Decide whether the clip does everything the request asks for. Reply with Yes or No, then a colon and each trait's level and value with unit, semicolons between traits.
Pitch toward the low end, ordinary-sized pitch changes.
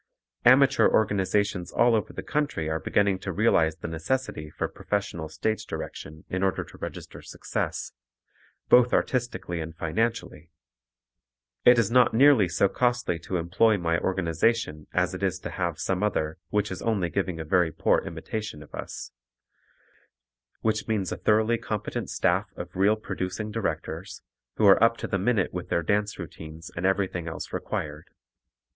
Yes: very low, 95 Hz; average, 4.7 semitones